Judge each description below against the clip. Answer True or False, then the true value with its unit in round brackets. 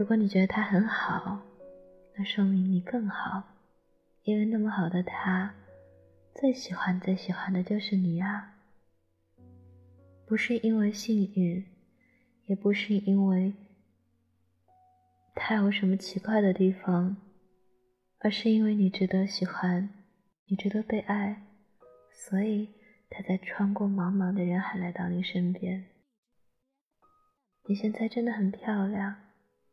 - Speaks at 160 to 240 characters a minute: True (180 characters per minute)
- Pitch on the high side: True (195 Hz)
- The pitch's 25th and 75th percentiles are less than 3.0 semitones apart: True (2.4 semitones)